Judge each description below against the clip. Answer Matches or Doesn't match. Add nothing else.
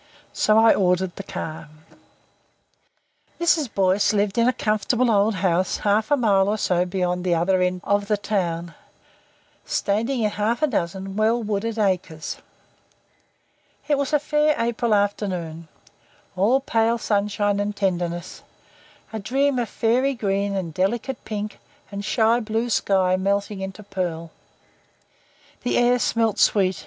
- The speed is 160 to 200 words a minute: Doesn't match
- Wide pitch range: Doesn't match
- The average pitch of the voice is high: Matches